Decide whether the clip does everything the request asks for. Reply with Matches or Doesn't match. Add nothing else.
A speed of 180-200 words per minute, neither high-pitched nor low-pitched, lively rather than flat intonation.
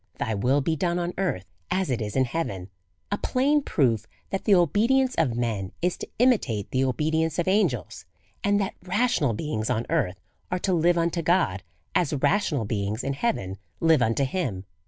Matches